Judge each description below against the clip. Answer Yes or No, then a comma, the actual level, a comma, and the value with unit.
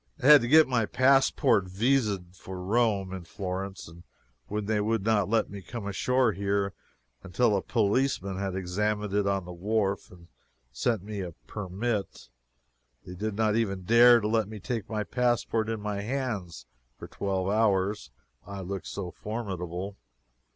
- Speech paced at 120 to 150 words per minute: No, average, 165 wpm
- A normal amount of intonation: Yes, average, 3.0 semitones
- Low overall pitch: Yes, low, 105 Hz